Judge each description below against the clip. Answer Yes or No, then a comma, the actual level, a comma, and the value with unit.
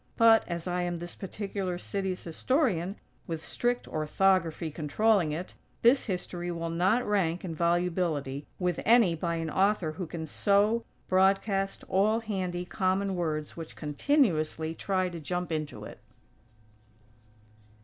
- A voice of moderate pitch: Yes, medium, 180 Hz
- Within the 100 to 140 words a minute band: Yes, slow, 135 wpm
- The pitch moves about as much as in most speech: Yes, average, 3.2 semitones